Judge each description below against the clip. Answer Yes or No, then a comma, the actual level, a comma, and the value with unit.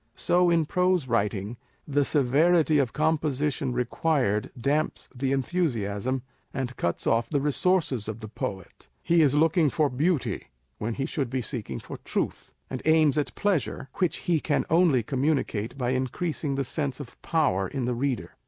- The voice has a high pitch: No, medium, 140 Hz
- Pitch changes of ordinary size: Yes, average, 4.4 semitones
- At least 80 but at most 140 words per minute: No, average, 160 wpm